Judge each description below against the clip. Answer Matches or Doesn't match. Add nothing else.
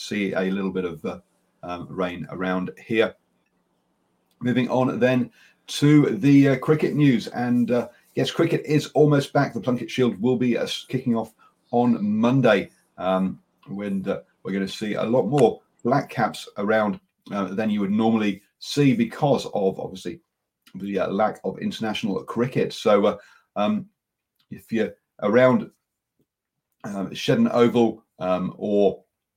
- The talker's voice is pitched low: Matches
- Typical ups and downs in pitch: Matches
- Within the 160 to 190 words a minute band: Doesn't match